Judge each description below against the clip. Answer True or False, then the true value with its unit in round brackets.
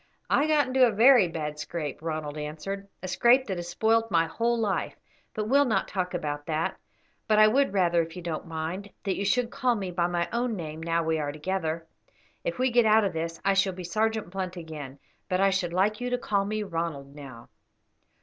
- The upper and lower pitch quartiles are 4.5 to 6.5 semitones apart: True (5.2 semitones)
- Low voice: False (185 Hz)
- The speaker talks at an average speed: False (220 wpm)